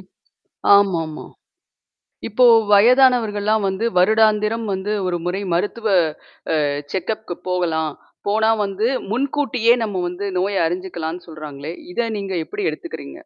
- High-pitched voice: Yes, high, 200 Hz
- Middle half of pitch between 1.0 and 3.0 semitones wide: No, average, 3.8 semitones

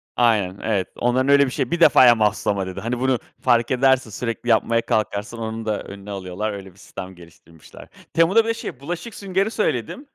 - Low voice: Yes, low, 115 Hz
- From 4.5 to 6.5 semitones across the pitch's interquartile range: Yes, average, 4.8 semitones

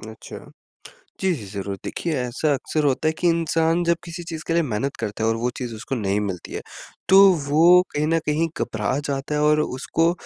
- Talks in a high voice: No, medium, 150 Hz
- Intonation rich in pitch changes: Yes, wide, 6.2 semitones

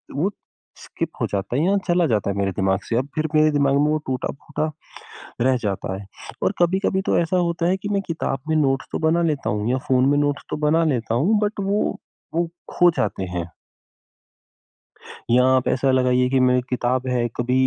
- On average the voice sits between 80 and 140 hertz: Yes, low, 135 Hz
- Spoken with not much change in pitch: No, average, 5.2 semitones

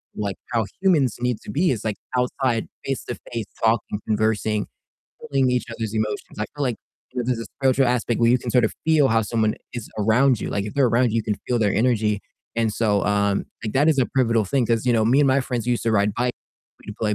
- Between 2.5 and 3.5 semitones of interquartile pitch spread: Yes, average, 2.8 semitones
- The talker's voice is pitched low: Yes, low, 115 Hz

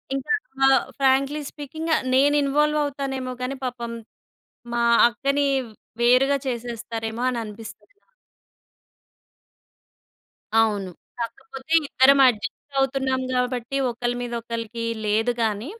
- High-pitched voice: Yes, very high, 255 Hz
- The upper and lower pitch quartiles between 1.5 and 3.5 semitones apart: Yes, average, 2.9 semitones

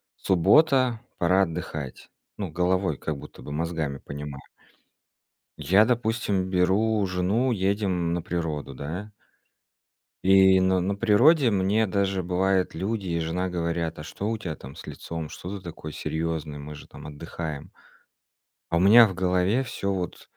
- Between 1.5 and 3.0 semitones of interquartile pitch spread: No, average, 3.6 semitones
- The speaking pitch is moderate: No, very low, 90 Hz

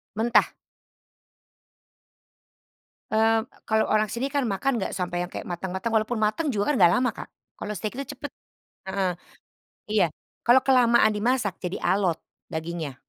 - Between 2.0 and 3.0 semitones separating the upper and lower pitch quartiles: No, average, 4.4 semitones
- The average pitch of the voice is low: No, high, 215 Hz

